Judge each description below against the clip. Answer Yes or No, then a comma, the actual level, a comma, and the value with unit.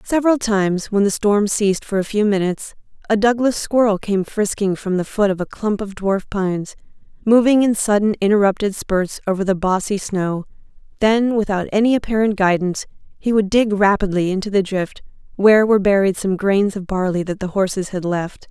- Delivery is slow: No, average, 185 wpm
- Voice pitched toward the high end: Yes, high, 200 Hz